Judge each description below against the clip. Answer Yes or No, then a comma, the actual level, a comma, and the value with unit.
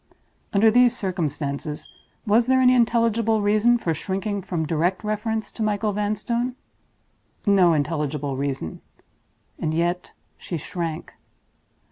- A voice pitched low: No, high, 200 Hz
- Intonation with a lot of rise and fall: Yes, wide, 5.7 semitones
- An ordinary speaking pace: No, slow, 110 wpm